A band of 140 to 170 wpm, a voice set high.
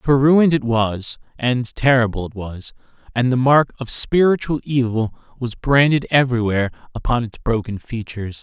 No: average, 150 wpm; low, 125 Hz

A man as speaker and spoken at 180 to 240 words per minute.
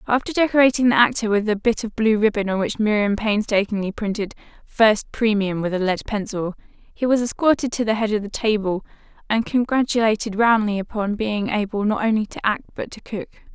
No: female; average, 190 wpm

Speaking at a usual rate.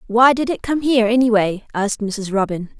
No: fast, 215 wpm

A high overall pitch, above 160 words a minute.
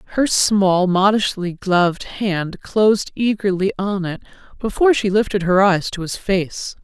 No: high, 195 Hz; average, 150 wpm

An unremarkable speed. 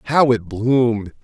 Yes: average, 145 wpm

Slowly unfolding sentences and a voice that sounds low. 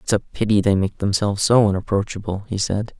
No: average, 200 wpm; low, 105 Hz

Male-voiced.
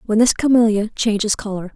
No: female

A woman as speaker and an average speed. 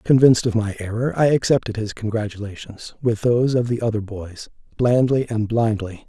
No: male; average, 170 wpm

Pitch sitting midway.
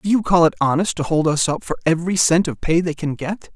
Yes: medium, 165 Hz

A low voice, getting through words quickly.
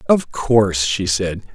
No: low, 100 Hz; average, 155 wpm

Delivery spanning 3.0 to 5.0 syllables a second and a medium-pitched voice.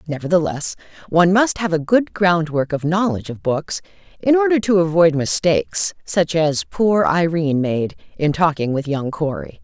Yes: 4.9 syllables/s; medium, 165 Hz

